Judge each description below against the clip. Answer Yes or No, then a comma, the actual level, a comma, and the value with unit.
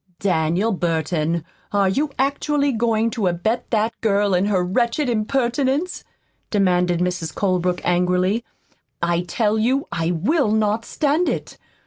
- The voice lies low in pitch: No, high, 205 Hz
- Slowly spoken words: Yes, slow, 130 wpm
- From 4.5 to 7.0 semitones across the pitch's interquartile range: Yes, average, 5.1 semitones